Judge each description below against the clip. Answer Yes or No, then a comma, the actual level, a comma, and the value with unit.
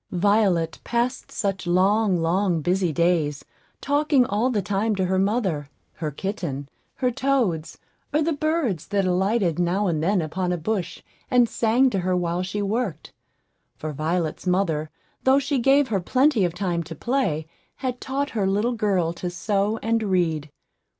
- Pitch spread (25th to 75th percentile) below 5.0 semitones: No, average, 5.3 semitones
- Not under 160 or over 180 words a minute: Yes, average, 165 wpm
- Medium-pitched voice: No, high, 195 Hz